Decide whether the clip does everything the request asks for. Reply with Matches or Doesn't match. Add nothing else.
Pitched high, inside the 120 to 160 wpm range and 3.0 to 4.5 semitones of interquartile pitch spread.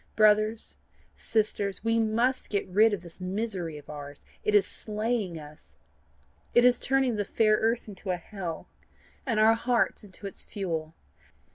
Matches